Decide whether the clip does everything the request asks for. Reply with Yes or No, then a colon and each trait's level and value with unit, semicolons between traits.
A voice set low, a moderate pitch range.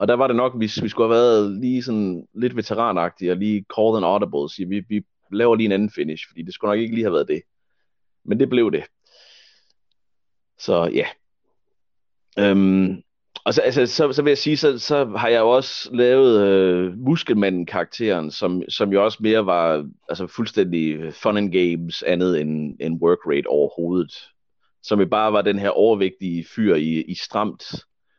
Yes: low, 100 Hz; average, 4.2 semitones